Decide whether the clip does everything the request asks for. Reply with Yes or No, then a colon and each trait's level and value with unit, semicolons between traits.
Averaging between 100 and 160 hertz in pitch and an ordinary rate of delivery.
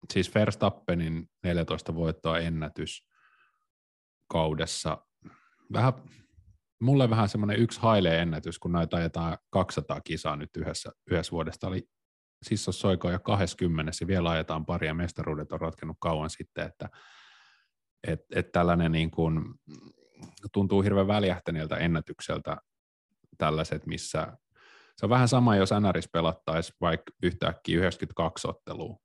No: very low, 85 Hz; average, 120 wpm